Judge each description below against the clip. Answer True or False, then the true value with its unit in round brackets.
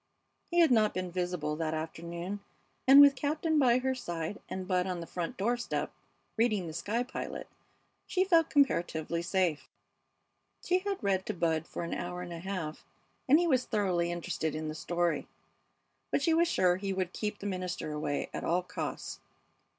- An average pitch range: False (6.4 semitones)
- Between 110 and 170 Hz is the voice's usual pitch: False (185 Hz)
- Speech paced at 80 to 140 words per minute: False (180 wpm)